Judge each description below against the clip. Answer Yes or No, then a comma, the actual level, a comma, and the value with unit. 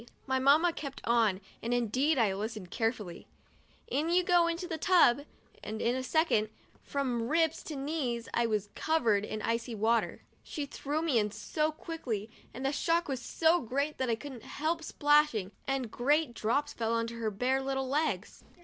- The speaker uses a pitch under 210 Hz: No, very high, 260 Hz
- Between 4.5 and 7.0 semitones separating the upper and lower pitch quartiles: Yes, average, 5.1 semitones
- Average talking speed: Yes, average, 175 wpm